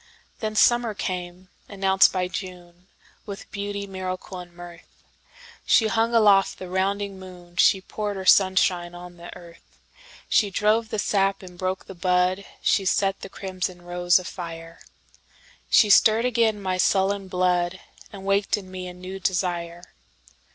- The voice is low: No, high, 190 Hz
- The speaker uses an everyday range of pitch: No, narrow, 2.1 semitones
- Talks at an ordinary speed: No, slow, 130 wpm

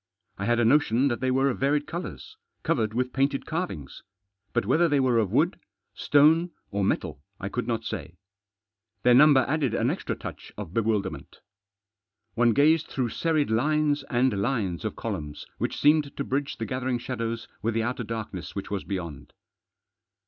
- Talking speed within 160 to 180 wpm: Yes, average, 170 wpm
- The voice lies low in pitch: Yes, low, 125 Hz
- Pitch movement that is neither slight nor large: Yes, average, 4.7 semitones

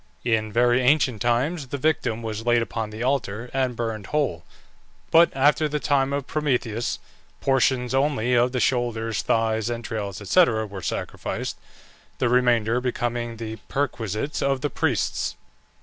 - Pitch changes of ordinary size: Yes, average, 3.2 semitones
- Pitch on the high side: No, low, 120 Hz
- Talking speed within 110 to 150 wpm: Yes, average, 145 wpm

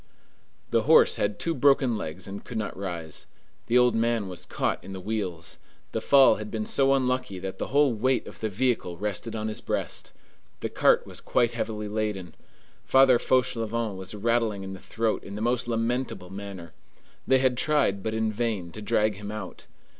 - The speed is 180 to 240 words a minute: Yes, average, 190 wpm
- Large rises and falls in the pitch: No, average, 3.7 semitones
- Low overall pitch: Yes, low, 110 Hz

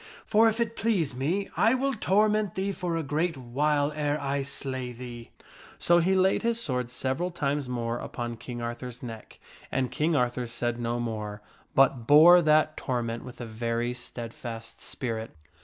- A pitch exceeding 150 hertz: No, low, 135 Hz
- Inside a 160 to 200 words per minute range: Yes, average, 170 wpm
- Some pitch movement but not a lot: No, wide, 6.3 semitones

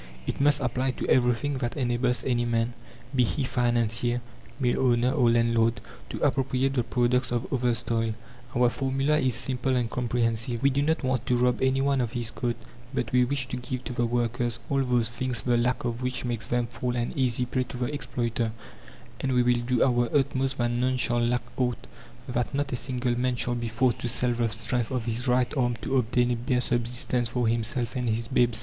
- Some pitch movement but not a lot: No, narrow, 1.4 semitones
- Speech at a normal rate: No, fast, 210 wpm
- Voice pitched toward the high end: No, low, 125 Hz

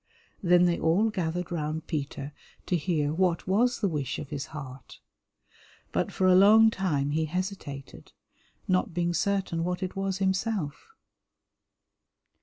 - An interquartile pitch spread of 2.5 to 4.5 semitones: Yes, average, 4.0 semitones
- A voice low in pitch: No, medium, 175 Hz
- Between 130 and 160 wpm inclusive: Yes, average, 140 wpm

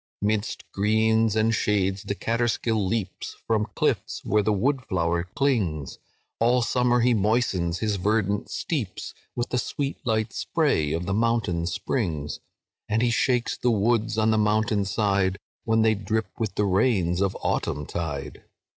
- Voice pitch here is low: Yes, low, 110 Hz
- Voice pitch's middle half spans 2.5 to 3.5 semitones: Yes, average, 3.1 semitones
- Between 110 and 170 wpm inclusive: Yes, average, 155 wpm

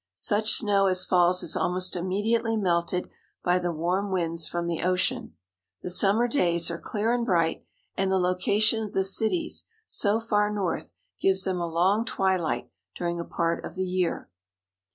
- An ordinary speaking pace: Yes, average, 170 wpm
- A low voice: No, medium, 185 Hz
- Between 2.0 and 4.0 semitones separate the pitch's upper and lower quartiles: Yes, average, 3.1 semitones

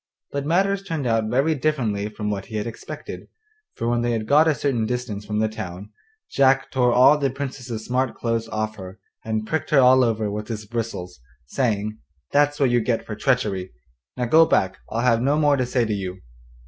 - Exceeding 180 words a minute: Yes, fast, 205 wpm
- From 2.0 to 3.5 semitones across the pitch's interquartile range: No, average, 3.9 semitones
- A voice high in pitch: No, low, 120 Hz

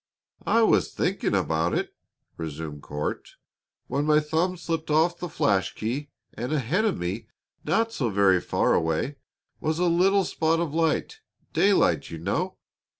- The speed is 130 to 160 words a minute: Yes, average, 150 wpm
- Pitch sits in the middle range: Yes, medium, 150 Hz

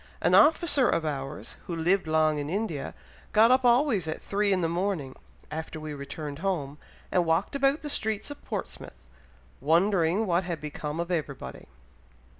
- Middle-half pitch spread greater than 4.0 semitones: Yes, average, 5.3 semitones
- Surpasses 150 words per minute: Yes, average, 165 wpm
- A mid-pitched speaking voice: Yes, medium, 170 Hz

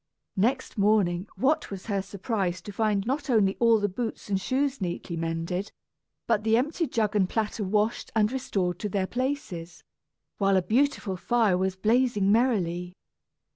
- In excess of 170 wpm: No, average, 160 wpm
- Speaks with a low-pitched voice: No, high, 210 Hz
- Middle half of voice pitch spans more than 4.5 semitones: No, average, 4.0 semitones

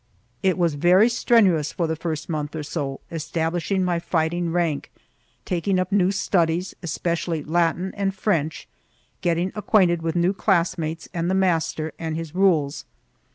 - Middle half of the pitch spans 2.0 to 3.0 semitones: Yes, narrow, 2.6 semitones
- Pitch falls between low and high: Yes, medium, 170 Hz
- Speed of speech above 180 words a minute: No, average, 150 wpm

